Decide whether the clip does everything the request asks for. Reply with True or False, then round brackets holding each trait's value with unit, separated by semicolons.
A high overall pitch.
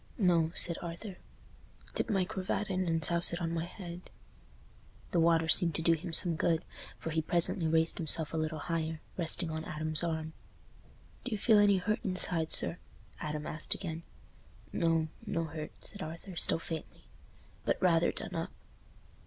False (165 Hz)